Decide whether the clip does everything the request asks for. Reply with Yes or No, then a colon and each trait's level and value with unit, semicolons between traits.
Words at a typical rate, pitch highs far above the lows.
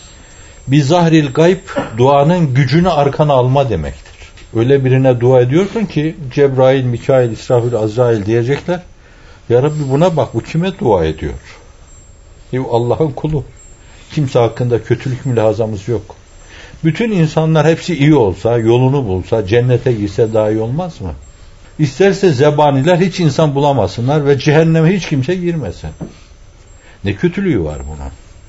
Yes: average, 125 wpm; wide, 6.7 semitones